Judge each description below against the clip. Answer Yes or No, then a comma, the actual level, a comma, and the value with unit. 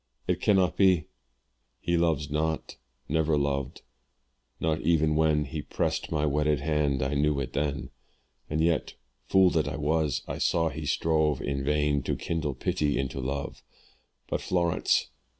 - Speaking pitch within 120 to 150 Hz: No, very low, 75 Hz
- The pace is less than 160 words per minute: Yes, average, 150 wpm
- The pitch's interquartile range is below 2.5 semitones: Yes, narrow, 2.0 semitones